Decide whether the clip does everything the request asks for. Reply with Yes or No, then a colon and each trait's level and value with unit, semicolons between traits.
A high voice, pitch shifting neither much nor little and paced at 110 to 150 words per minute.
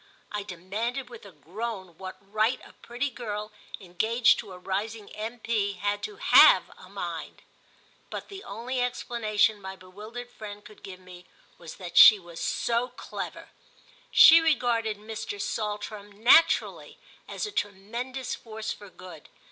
Yes: high, 215 Hz; average, 3.2 semitones; average, 145 wpm